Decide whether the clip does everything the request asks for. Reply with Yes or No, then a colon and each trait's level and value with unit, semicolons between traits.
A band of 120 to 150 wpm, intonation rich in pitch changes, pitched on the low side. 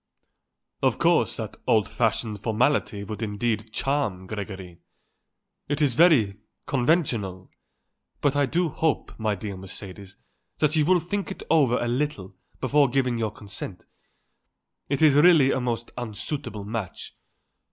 Yes: average, 140 wpm; wide, 5.8 semitones; low, 120 Hz